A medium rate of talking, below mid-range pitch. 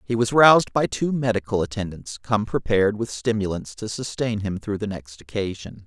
Yes: average, 185 wpm; low, 110 Hz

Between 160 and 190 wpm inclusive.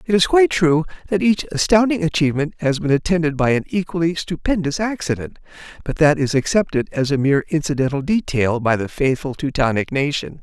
Yes: average, 175 wpm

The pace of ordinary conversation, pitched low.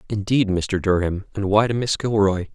Yes: average, 190 wpm; low, 100 Hz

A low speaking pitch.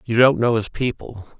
Yes: low, 115 Hz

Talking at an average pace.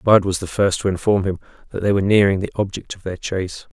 No: fast, 255 wpm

